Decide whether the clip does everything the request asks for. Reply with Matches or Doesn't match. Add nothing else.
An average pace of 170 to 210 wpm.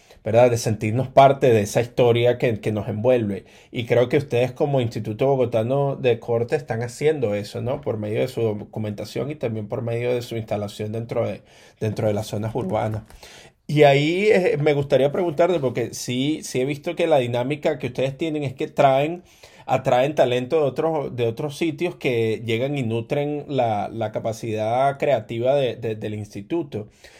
Matches